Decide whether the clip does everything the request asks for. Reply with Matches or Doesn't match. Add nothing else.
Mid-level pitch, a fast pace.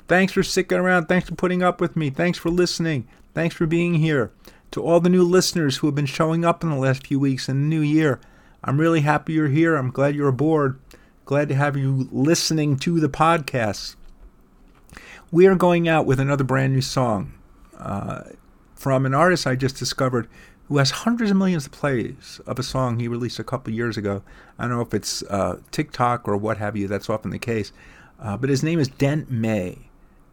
Matches